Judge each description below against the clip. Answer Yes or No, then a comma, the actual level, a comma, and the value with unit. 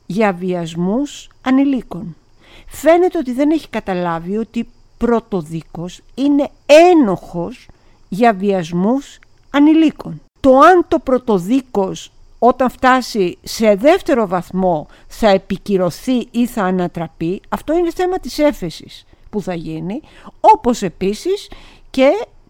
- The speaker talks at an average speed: No, slow, 105 wpm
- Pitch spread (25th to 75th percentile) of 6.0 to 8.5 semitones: Yes, wide, 7.1 semitones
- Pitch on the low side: No, high, 225 Hz